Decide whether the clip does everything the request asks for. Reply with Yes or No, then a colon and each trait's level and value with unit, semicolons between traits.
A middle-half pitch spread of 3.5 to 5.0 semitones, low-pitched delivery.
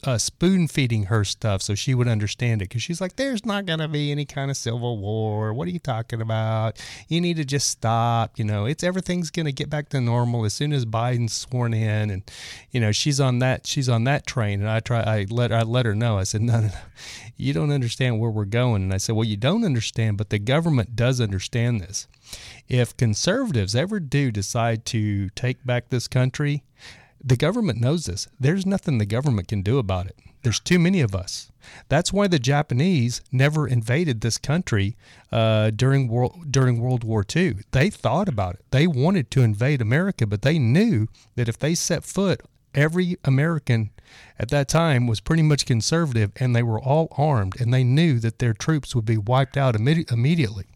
Yes: average, 4.6 semitones; low, 125 Hz